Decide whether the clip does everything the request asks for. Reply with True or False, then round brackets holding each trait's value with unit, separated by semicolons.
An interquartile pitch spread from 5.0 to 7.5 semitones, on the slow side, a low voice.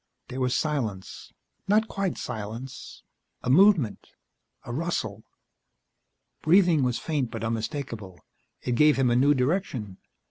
True (5.6 semitones; 120 wpm; 130 Hz)